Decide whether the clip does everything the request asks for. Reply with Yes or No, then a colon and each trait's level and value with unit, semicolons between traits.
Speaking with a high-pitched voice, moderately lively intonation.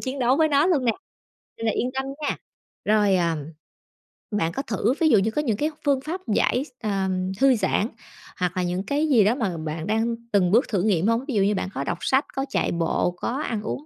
No: high, 225 Hz; wide, 5.7 semitones